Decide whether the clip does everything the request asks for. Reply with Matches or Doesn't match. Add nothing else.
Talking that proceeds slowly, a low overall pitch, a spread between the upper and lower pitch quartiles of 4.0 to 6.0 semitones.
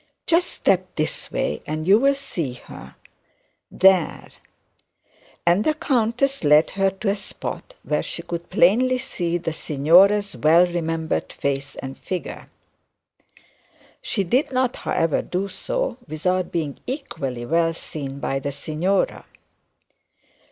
Doesn't match